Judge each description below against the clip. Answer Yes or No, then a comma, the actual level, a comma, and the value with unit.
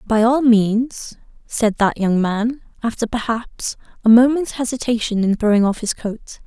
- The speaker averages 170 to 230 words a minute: No, average, 160 wpm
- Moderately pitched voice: No, high, 230 Hz